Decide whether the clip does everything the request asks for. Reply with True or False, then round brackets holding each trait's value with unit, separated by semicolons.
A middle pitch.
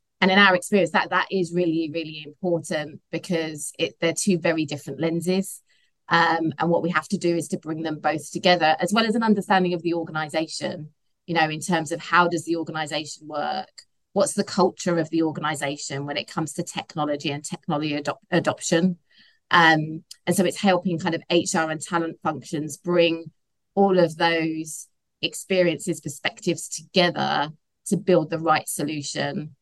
True (165 Hz)